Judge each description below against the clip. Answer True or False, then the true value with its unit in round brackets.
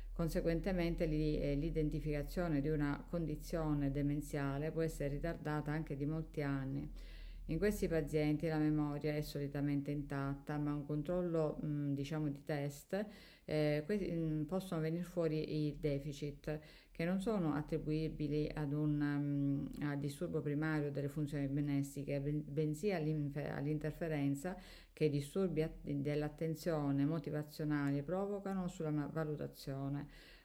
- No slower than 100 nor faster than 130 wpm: True (120 wpm)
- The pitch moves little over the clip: True (1.9 semitones)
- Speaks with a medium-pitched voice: True (150 Hz)